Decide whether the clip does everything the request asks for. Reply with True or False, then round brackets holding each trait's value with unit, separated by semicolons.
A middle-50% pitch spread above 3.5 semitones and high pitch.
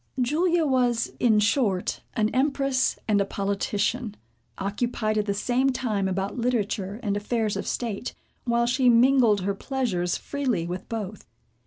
True (3.9 semitones; 225 Hz)